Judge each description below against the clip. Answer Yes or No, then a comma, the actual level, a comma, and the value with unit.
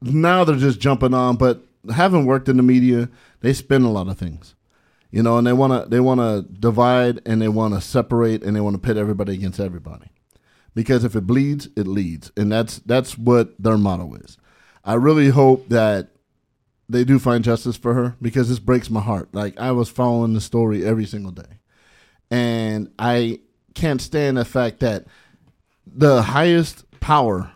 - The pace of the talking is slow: No, average, 190 wpm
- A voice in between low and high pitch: No, low, 120 Hz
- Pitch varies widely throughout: No, average, 3.4 semitones